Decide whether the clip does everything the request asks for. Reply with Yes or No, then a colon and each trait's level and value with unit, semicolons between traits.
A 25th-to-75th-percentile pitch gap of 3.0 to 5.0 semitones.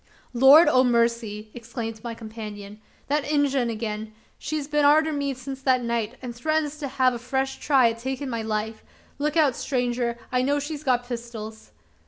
Yes: average, 3.6 semitones